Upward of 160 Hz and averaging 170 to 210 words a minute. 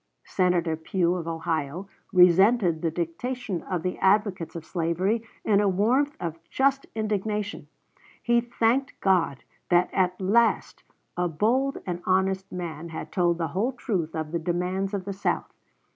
No: medium, 185 Hz; average, 150 wpm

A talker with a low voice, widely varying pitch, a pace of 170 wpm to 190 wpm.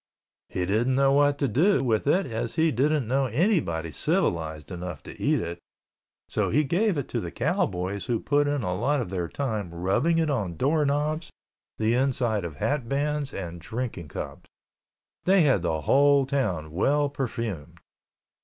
Yes: low, 125 Hz; wide, 7.9 semitones; average, 175 wpm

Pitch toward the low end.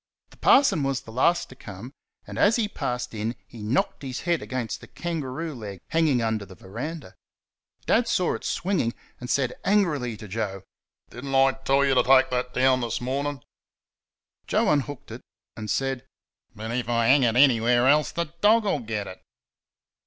Yes: low, 130 Hz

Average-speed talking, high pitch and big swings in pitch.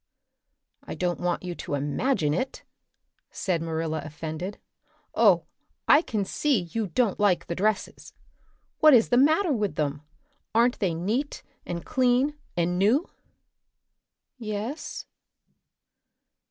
No: slow, 120 wpm; high, 200 Hz; wide, 6.7 semitones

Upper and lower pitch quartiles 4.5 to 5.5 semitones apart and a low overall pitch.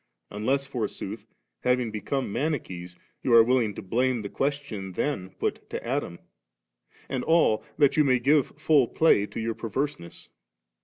Yes: average, 4.8 semitones; low, 125 Hz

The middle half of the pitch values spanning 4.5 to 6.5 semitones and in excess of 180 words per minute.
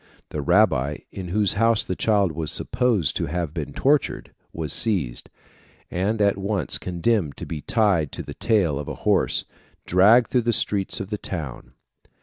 No: average, 5.3 semitones; average, 175 wpm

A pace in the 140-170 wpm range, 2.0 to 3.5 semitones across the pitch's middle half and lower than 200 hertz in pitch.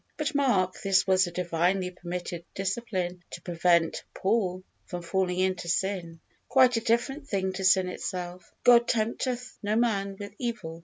No: average, 155 wpm; average, 4.2 semitones; high, 190 Hz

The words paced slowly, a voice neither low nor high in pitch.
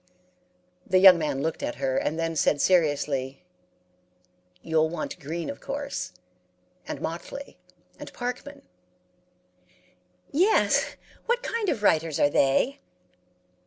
Yes: slow, 115 wpm; medium, 165 Hz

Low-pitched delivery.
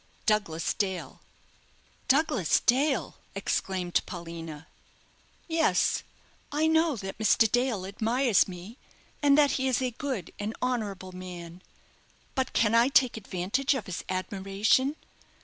No: high, 215 Hz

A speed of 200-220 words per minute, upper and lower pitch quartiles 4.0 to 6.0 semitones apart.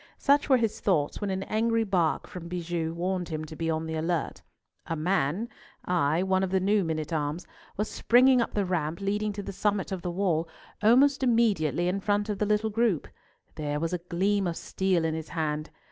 Yes: fast, 205 wpm; average, 4.3 semitones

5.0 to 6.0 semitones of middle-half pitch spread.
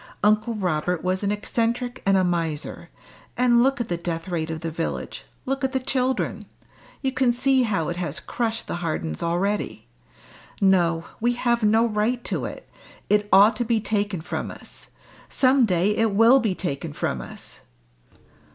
Yes: wide, 5.5 semitones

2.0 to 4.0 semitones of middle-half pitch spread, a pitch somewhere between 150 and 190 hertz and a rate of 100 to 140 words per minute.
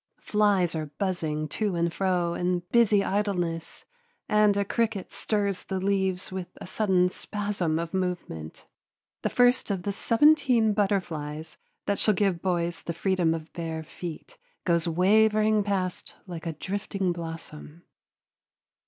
Yes: average, 3.4 semitones; medium, 185 Hz; slow, 135 wpm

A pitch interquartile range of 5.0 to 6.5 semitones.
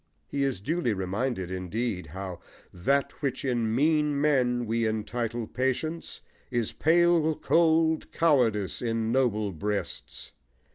Yes: wide, 5.6 semitones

